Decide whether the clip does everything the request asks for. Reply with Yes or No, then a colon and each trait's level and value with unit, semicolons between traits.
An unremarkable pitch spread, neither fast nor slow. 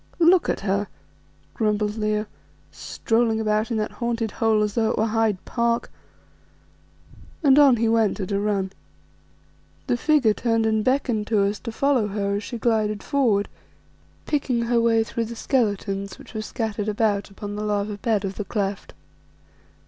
No: narrow, 2.1 semitones; average, 165 wpm